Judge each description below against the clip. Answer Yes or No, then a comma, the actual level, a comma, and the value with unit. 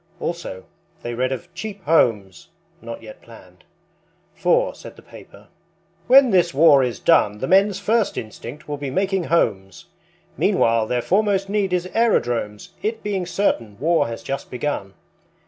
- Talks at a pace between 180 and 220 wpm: No, average, 150 wpm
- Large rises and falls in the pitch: Yes, wide, 8.9 semitones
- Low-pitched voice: No, medium, 145 Hz